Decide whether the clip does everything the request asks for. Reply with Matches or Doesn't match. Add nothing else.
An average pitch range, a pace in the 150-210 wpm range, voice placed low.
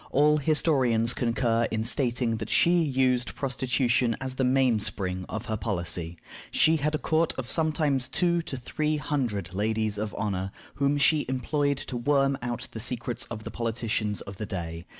Matches